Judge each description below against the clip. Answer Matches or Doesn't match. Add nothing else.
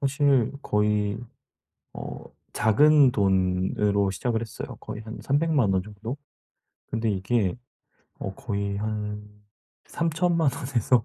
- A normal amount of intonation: Matches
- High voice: Doesn't match